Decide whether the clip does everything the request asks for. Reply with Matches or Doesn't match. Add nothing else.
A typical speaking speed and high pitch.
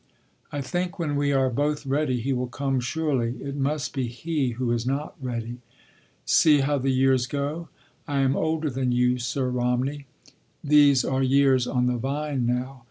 Doesn't match